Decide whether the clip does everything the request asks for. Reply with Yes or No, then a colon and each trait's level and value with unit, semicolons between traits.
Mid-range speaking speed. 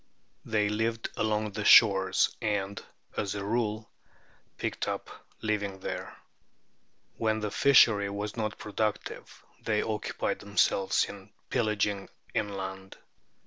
No: slow, 115 wpm